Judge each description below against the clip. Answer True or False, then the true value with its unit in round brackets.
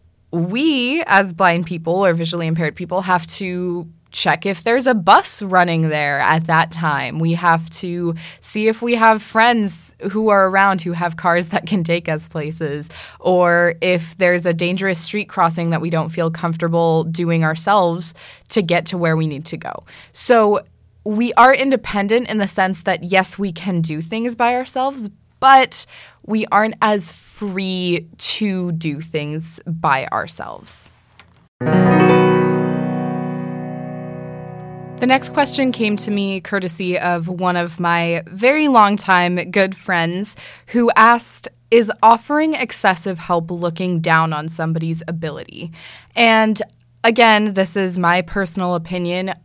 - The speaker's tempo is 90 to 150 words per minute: True (145 wpm)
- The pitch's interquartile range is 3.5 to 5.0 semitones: True (3.9 semitones)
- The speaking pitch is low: False (180 Hz)